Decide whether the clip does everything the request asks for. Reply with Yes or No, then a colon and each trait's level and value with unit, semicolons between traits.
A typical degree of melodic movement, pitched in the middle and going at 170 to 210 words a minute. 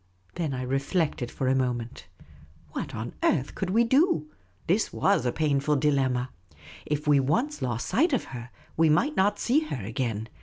No: wide, 6.9 semitones; medium, 145 Hz; average, 175 wpm